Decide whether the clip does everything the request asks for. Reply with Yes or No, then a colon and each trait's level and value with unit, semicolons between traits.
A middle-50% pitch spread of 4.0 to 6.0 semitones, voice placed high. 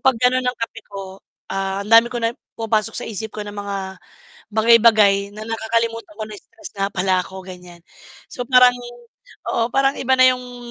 No: average, 3.3 semitones; high, 220 Hz